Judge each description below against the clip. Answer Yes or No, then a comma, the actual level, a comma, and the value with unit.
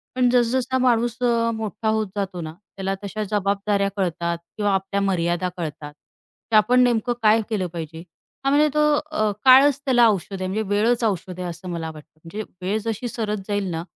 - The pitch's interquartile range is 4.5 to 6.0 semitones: No, average, 4.1 semitones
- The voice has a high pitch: Yes, high, 205 Hz